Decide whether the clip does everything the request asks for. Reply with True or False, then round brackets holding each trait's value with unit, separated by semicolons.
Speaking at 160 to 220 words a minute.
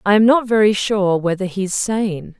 True (200 wpm)